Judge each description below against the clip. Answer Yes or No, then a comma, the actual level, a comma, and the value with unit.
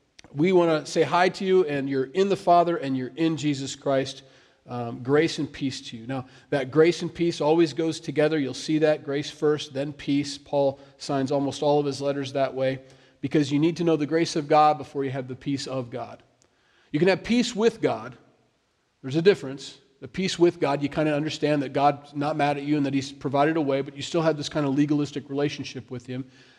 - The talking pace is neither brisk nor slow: No, fast, 230 wpm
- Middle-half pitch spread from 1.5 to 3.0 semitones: Yes, average, 2.7 semitones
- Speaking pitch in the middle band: Yes, medium, 145 Hz